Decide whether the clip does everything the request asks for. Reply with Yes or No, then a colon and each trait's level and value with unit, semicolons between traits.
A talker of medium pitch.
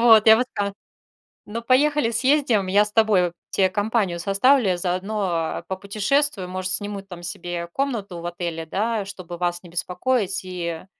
No: high, 195 Hz